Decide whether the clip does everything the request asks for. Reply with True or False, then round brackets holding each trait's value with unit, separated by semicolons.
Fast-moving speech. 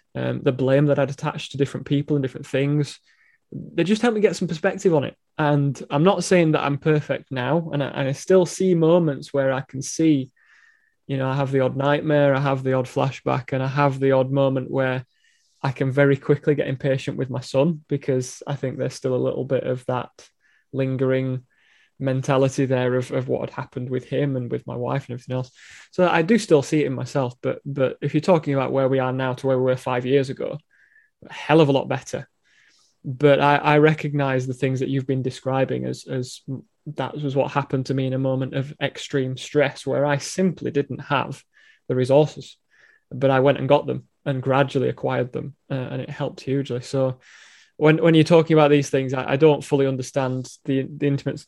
True (220 wpm)